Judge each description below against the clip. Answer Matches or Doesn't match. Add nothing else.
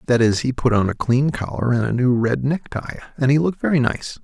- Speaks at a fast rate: Matches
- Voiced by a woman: Doesn't match